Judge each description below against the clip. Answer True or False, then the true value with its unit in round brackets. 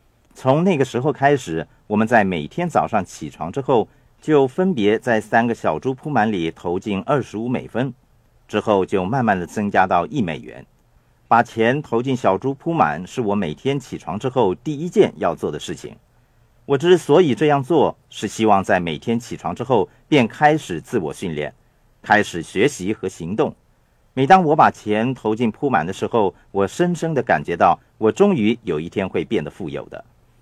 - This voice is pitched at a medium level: False (125 Hz)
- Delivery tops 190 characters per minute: True (265 characters per minute)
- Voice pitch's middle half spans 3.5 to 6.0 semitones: True (5.4 semitones)